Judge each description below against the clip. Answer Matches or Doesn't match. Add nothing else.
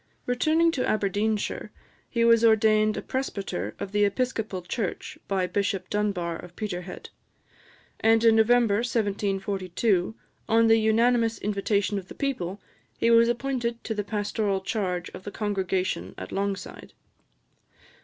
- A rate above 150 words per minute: Doesn't match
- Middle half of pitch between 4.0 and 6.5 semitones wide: Doesn't match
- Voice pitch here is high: Matches